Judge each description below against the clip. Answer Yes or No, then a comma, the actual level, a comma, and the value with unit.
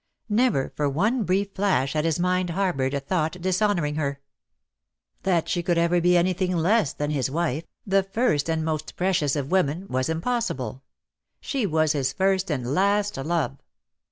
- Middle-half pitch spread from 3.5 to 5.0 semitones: Yes, average, 4.5 semitones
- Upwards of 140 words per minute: Yes, average, 165 wpm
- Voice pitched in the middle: Yes, medium, 170 Hz